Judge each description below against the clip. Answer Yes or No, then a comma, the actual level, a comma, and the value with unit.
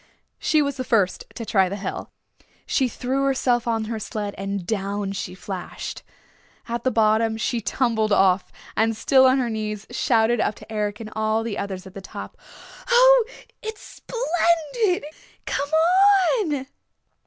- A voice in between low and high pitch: No, high, 225 Hz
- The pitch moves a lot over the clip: No, average, 4.6 semitones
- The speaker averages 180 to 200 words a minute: No, average, 155 wpm